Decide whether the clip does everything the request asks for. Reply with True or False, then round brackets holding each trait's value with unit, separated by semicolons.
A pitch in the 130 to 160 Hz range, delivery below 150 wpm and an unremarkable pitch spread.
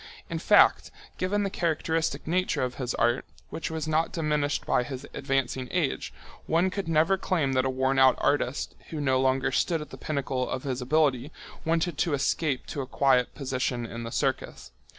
False (140 Hz; 185 wpm; 3.7 semitones)